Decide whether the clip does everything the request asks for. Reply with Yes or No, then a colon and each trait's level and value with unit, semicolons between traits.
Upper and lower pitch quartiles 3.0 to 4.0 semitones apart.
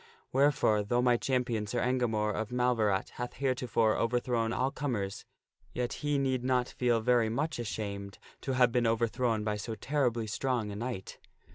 No: narrow, 2.6 semitones